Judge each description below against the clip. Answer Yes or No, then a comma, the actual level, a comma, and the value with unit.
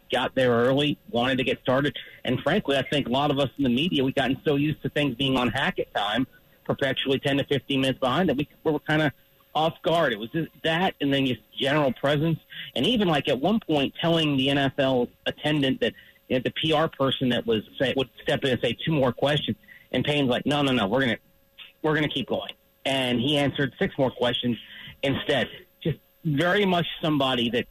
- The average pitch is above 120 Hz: Yes, medium, 140 Hz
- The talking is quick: Yes, fast, 225 wpm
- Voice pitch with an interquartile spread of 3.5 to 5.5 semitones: No, narrow, 2.5 semitones